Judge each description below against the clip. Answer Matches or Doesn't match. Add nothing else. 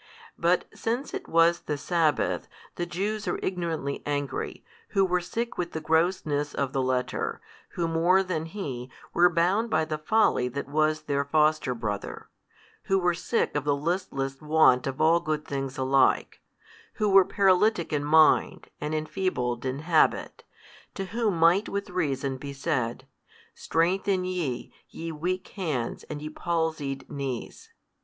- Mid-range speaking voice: Matches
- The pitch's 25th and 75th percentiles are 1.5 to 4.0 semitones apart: Doesn't match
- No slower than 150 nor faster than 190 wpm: Matches